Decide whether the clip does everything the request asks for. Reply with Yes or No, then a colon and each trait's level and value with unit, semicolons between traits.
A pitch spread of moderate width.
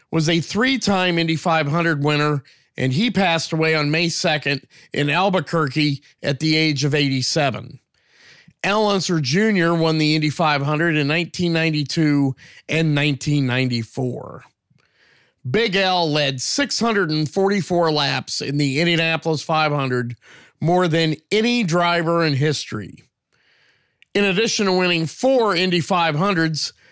Yes: average, 3.5 semitones